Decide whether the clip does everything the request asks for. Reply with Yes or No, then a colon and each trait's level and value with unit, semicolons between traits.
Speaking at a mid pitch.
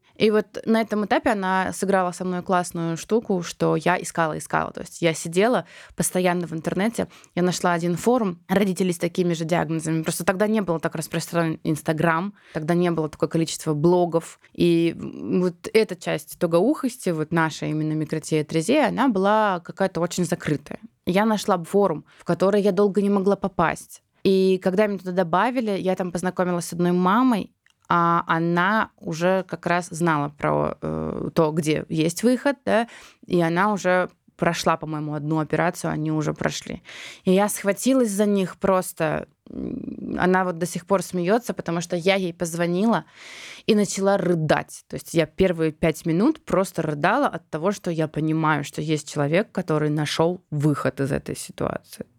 Yes: medium, 175 Hz